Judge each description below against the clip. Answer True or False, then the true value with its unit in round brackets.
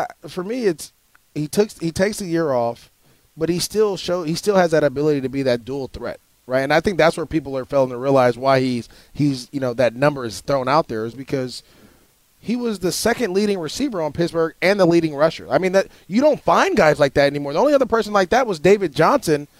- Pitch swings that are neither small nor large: False (5.8 semitones)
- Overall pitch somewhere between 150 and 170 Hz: True (160 Hz)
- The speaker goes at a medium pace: False (240 wpm)